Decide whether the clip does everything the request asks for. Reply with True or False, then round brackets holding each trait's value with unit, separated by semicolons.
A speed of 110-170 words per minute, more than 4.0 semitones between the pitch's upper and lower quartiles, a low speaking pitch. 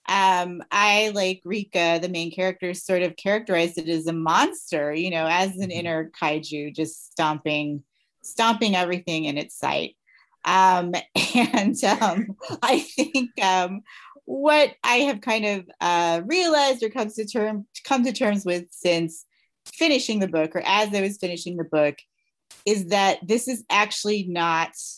False (155 wpm; 4.6 semitones; 190 Hz)